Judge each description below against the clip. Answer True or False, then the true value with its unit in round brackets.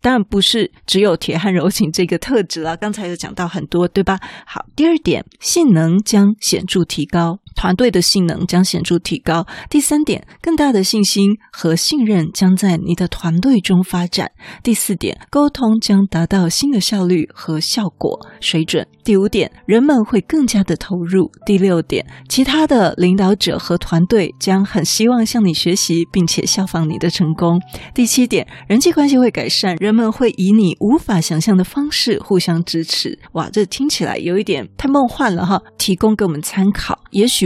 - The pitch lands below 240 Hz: True (190 Hz)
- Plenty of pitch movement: False (4.2 semitones)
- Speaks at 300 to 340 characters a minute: False (270 characters per minute)